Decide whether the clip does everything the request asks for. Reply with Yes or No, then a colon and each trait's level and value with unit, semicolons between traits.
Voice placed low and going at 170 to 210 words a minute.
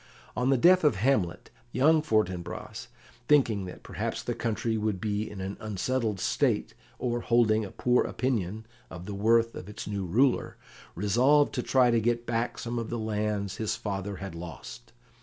Yes: low, 110 Hz; average, 175 wpm